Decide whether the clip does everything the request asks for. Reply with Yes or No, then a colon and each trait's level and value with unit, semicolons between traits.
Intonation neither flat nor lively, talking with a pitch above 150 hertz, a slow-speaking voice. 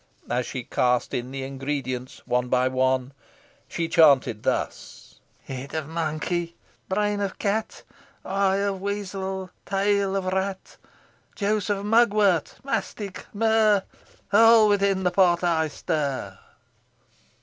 No: wide, 6.6 semitones; medium, 185 Hz; slow, 120 wpm